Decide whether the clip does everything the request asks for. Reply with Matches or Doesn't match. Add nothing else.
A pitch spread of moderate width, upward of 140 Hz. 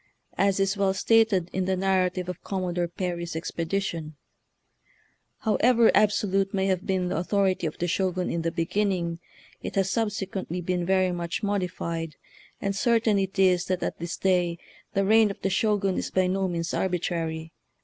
Doesn't match